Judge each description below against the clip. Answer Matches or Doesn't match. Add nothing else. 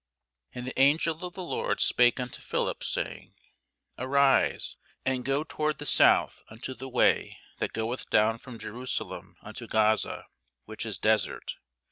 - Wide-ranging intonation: Doesn't match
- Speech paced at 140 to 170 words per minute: Matches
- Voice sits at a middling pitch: Doesn't match